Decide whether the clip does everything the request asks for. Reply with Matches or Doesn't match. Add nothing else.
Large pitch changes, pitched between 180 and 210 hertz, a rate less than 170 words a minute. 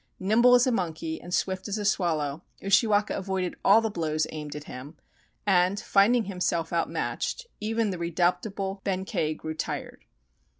Doesn't match